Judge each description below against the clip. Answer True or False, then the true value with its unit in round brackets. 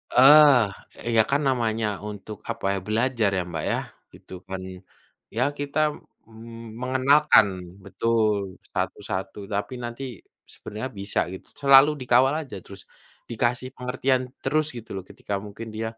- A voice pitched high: False (115 Hz)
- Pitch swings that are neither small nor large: True (3.8 semitones)